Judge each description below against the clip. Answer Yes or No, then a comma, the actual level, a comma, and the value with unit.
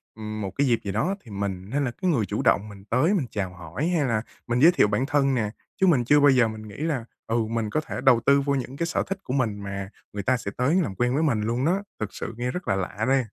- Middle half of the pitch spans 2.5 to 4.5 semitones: No, wide, 5.4 semitones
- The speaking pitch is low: Yes, low, 125 Hz